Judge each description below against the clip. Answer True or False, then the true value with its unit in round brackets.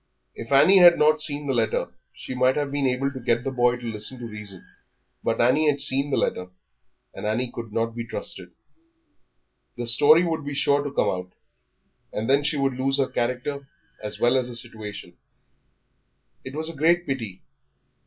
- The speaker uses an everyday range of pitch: True (3.5 semitones)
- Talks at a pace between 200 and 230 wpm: False (190 wpm)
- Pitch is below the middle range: True (130 Hz)